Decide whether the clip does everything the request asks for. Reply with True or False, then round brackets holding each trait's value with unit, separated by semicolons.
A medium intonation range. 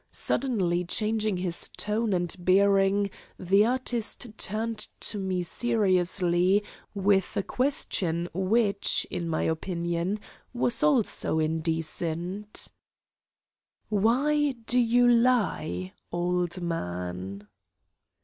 True (4.5 semitones)